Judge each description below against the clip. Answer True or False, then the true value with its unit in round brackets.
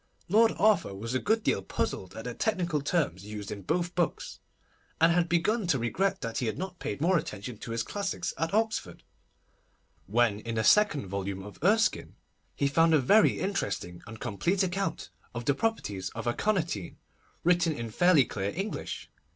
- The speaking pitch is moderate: True (160 Hz)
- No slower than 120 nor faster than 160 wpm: False (175 wpm)